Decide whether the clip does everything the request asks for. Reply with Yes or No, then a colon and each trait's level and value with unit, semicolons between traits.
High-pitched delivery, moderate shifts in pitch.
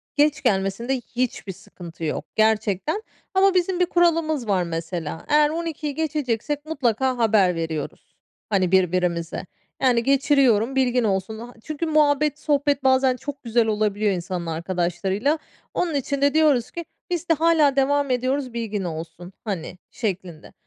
No: high, 245 Hz; wide, 7.3 semitones